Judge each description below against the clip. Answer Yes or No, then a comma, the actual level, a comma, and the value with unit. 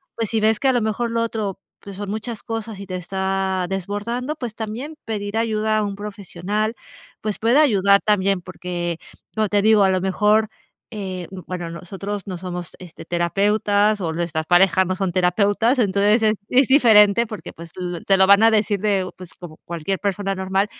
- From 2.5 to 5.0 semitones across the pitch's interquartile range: Yes, average, 2.8 semitones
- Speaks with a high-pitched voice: Yes, high, 200 Hz